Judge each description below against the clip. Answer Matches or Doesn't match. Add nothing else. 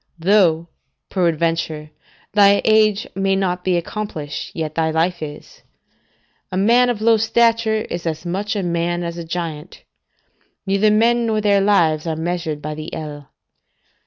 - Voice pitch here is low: Doesn't match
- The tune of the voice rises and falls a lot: Doesn't match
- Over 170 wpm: Doesn't match